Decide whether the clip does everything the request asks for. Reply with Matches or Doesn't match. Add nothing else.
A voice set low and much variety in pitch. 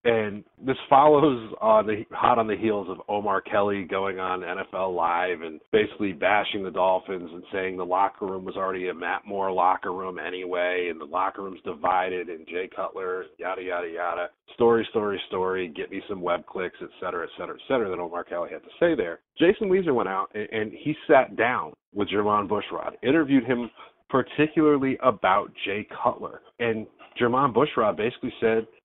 Matches